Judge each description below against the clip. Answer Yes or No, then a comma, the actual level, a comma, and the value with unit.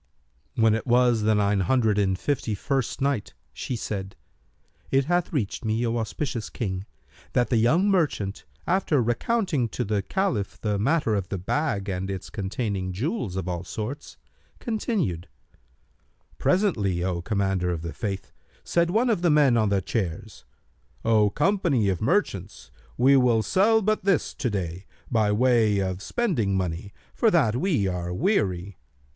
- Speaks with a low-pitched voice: Yes, low, 110 Hz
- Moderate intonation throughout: No, wide, 6.7 semitones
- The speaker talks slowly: No, average, 155 wpm